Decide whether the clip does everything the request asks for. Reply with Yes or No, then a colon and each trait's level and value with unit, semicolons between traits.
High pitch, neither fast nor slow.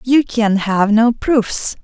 Yes: high, 230 Hz; average, 165 wpm